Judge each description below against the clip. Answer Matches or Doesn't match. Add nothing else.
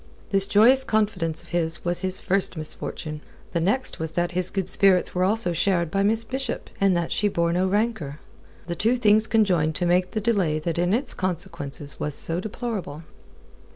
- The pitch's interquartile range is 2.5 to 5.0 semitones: Matches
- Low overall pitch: Doesn't match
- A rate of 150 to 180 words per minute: Doesn't match